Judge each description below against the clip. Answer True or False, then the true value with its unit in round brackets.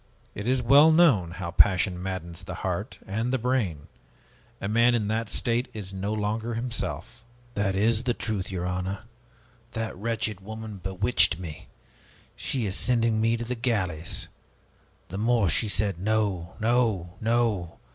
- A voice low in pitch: True (110 Hz)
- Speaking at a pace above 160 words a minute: False (155 wpm)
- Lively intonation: False (3.7 semitones)